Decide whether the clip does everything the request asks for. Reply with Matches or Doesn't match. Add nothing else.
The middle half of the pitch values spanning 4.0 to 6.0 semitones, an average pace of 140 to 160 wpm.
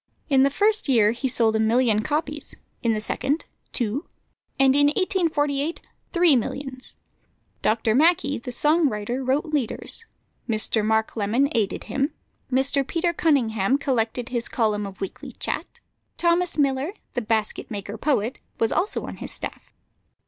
Matches